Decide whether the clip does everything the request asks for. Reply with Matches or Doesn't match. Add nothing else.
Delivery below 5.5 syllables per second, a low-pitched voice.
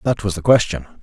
Doesn't match